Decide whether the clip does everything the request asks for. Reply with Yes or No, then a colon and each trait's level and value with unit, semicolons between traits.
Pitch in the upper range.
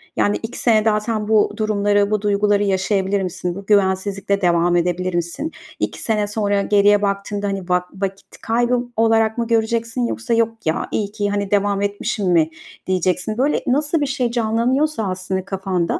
Yes: high, 205 Hz